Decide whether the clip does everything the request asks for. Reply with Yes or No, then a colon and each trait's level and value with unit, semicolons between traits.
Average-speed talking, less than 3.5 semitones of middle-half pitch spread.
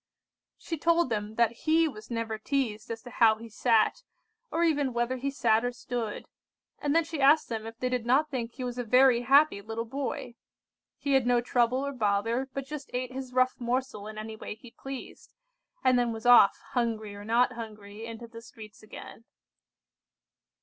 Yes: average, 190 wpm; average, 2.9 semitones